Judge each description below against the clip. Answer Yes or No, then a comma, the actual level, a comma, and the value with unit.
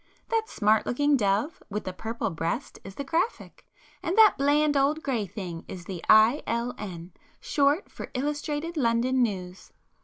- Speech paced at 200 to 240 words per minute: No, average, 160 wpm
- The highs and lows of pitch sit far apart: Yes, wide, 6.7 semitones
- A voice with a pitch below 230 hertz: No, high, 245 Hz